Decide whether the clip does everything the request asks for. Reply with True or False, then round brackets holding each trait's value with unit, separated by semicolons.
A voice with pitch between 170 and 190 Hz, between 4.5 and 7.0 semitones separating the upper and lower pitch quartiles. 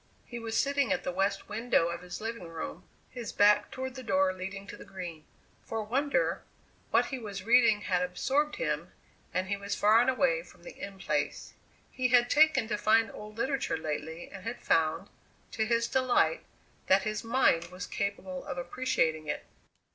False (210 Hz; 5.1 semitones)